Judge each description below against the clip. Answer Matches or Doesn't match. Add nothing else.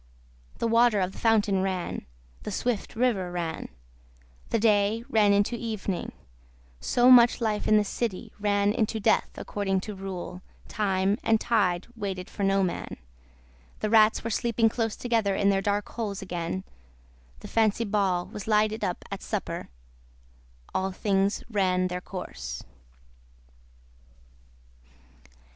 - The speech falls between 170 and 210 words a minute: Doesn't match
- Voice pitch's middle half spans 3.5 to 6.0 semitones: Doesn't match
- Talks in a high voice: Matches